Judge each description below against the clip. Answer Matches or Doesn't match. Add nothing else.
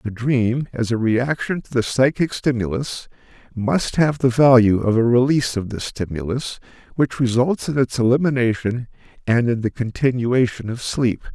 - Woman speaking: Doesn't match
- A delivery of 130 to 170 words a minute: Matches